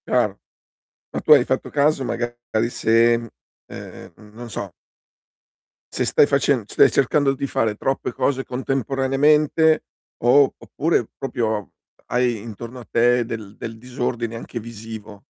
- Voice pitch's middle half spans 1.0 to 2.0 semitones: No, average, 2.9 semitones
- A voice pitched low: Yes, low, 120 Hz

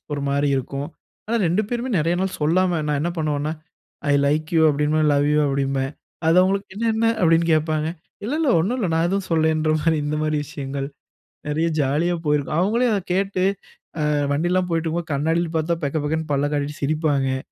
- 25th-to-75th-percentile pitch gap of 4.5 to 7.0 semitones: No, average, 3.2 semitones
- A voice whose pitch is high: No, medium, 155 Hz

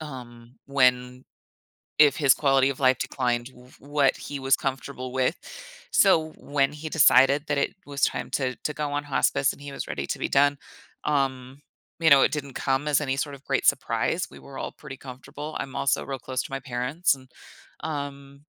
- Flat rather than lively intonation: Yes, narrow, 1.8 semitones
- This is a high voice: No, low, 135 Hz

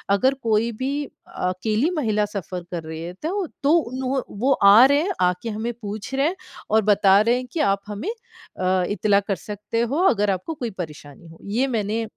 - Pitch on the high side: Yes, high, 215 Hz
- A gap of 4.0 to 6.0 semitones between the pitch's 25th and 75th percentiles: Yes, average, 4.7 semitones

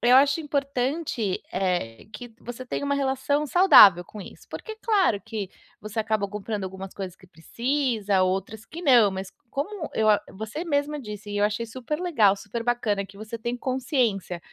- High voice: Yes, high, 225 Hz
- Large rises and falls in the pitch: Yes, wide, 5.7 semitones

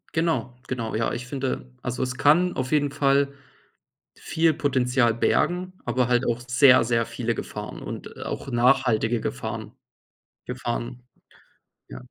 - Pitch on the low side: Yes, low, 125 Hz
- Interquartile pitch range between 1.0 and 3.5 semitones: Yes, average, 2.9 semitones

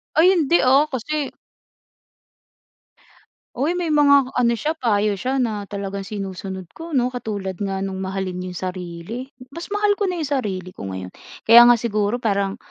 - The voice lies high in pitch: Yes, high, 230 Hz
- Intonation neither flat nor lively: No, wide, 6.5 semitones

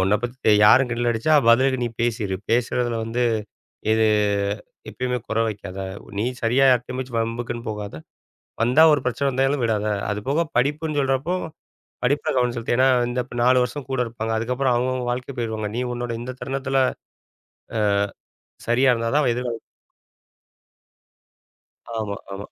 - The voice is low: Yes, low, 120 Hz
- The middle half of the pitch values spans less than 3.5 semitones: Yes, narrow, 2.4 semitones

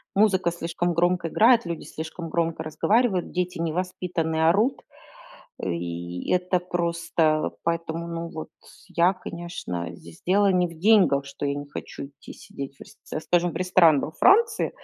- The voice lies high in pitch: No, medium, 170 Hz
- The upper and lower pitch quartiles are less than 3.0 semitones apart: Yes, narrow, 2.5 semitones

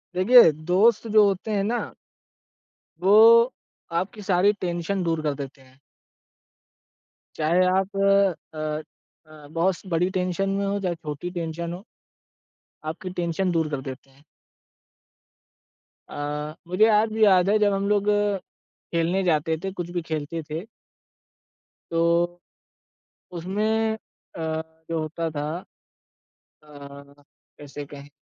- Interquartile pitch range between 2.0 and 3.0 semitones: No, average, 4.1 semitones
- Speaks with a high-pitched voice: No, medium, 175 Hz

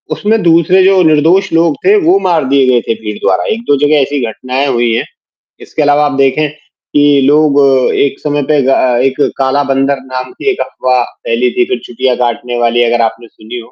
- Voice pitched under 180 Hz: Yes, medium, 140 Hz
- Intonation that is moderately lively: Yes, average, 3.9 semitones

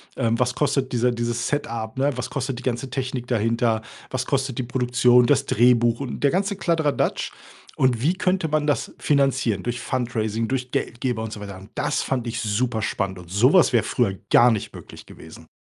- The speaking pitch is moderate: No, low, 125 Hz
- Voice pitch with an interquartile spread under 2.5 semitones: No, average, 2.8 semitones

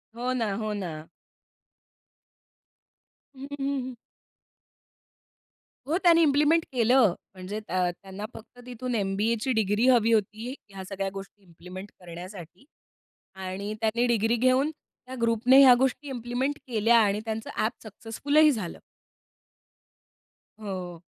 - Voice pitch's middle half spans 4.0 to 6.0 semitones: Yes, average, 4.5 semitones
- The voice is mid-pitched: No, high, 225 Hz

